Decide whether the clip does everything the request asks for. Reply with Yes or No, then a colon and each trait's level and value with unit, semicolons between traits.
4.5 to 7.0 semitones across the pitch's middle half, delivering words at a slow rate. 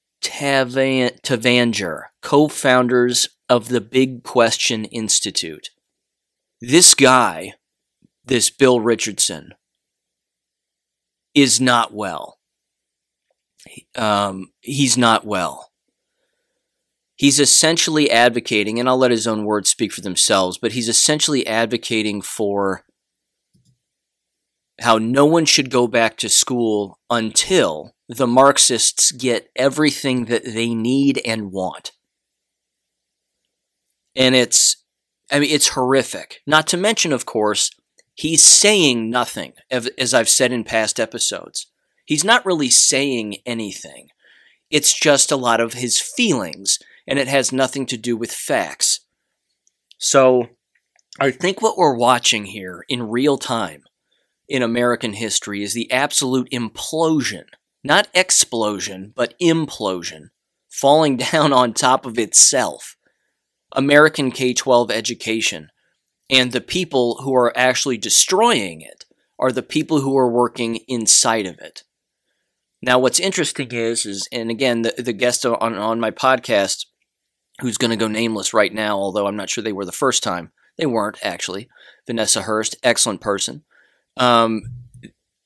No: average, 3.3 semitones; slow, 125 wpm